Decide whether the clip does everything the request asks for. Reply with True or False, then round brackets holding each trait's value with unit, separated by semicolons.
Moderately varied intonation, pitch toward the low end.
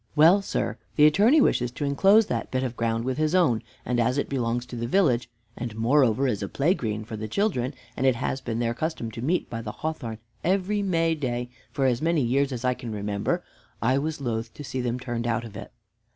True (4.7 semitones; 125 Hz)